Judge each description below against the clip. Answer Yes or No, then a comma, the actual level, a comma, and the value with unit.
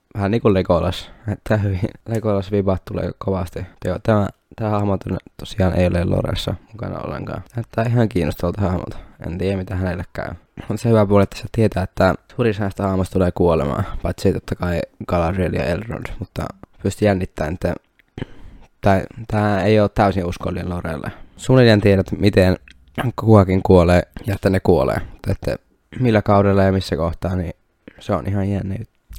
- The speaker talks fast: Yes, fast, 160 wpm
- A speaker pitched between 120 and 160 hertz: No, very low, 95 Hz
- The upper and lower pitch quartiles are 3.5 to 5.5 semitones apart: No, average, 2.9 semitones